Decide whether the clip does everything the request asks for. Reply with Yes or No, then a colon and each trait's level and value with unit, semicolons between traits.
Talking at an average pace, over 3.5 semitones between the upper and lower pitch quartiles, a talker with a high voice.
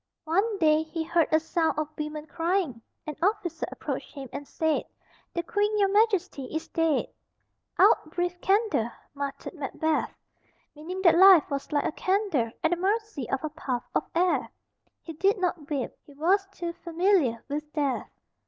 Yes: average, 165 wpm; average, 3.9 semitones; very high, 325 Hz